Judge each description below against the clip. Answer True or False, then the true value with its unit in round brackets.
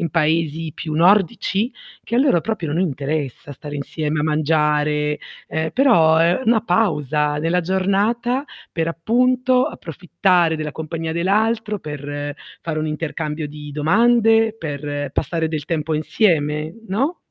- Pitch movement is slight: False (5.1 semitones)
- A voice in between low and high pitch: True (160 Hz)